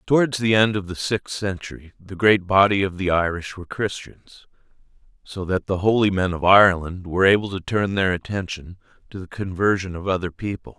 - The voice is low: Yes, very low, 95 Hz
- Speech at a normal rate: Yes, average, 190 wpm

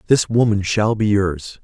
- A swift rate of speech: No, average, 185 wpm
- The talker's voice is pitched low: Yes, low, 105 Hz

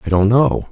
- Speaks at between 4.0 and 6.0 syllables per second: Yes, 5.1 syllables/s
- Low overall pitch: Yes, low, 100 Hz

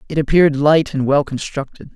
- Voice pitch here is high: No, medium, 145 Hz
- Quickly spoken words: No, average, 185 wpm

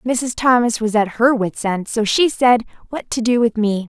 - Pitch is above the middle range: Yes, high, 230 Hz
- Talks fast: Yes, fast, 225 wpm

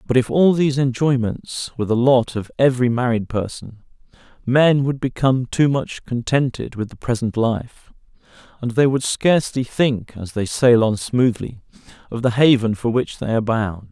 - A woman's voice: No, male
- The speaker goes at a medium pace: Yes, average, 170 wpm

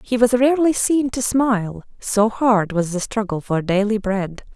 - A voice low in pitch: No, high, 220 Hz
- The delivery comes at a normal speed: Yes, average, 185 wpm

